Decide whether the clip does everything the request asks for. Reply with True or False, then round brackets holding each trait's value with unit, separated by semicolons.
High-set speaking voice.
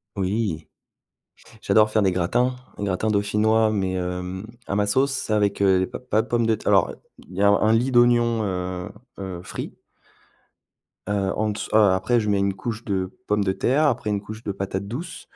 False (105 Hz)